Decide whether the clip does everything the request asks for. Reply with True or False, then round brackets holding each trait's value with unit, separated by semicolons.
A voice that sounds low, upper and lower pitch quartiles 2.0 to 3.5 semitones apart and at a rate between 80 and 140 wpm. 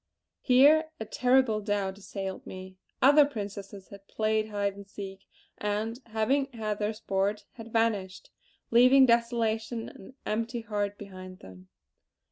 False (215 Hz; 2.8 semitones; 135 wpm)